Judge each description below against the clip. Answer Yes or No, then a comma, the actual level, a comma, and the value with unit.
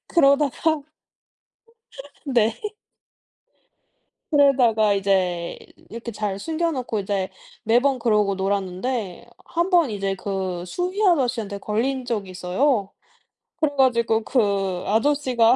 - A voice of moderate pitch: No, high, 225 Hz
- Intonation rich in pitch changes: Yes, wide, 5.7 semitones